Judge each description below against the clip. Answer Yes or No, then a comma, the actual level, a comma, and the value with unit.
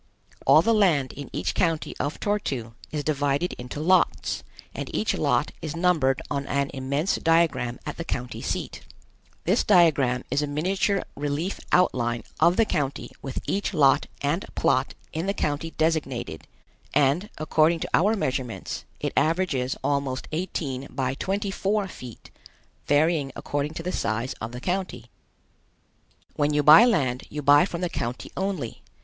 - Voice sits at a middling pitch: Yes, medium, 150 Hz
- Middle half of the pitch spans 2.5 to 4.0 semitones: No, average, 4.8 semitones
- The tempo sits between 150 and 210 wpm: Yes, average, 155 wpm